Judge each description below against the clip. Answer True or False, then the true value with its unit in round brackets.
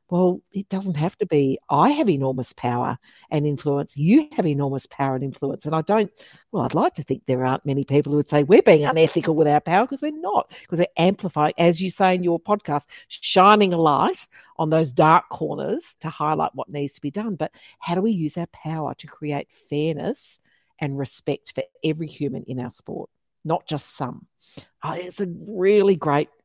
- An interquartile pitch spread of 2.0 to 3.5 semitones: False (4.4 semitones)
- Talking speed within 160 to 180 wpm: False (205 wpm)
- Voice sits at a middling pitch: True (160 Hz)